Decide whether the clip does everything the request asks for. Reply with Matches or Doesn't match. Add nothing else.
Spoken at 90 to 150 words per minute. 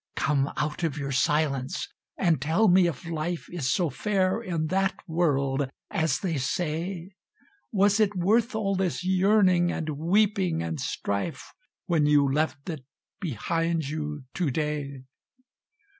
Matches